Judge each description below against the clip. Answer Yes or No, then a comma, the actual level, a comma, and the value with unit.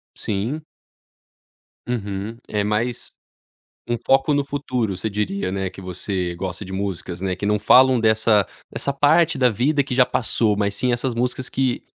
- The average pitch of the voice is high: No, low, 110 Hz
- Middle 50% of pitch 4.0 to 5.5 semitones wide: Yes, average, 4.6 semitones